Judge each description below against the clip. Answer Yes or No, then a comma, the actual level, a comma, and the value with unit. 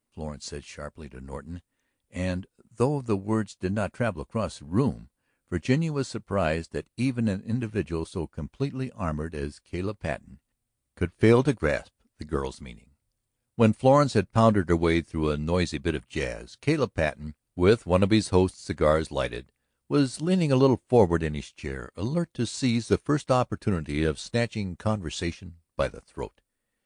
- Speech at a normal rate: Yes, average, 170 wpm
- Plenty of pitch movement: Yes, wide, 7.0 semitones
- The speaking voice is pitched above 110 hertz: No, very low, 95 Hz